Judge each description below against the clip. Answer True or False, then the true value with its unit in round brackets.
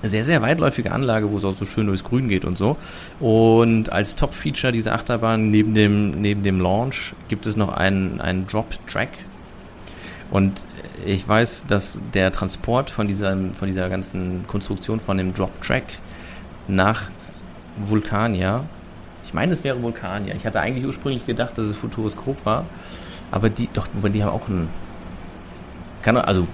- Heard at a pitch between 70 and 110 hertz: True (105 Hz)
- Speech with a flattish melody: False (3.0 semitones)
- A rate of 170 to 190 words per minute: False (160 wpm)